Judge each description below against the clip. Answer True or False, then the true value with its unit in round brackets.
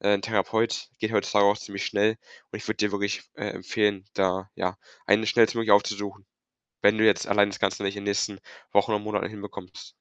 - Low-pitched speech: True (100 Hz)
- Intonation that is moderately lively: False (1.4 semitones)